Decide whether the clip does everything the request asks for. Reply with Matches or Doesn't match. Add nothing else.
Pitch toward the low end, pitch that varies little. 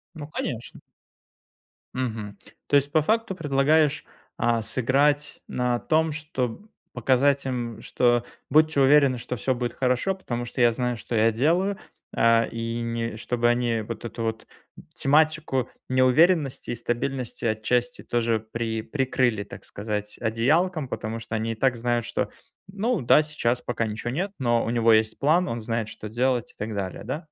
Doesn't match